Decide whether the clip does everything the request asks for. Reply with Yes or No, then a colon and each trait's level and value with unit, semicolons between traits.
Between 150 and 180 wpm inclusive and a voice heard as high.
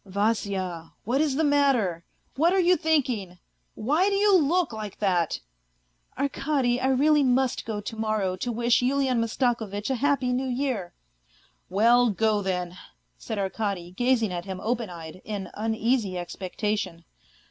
Yes: average, 170 wpm; high, 225 Hz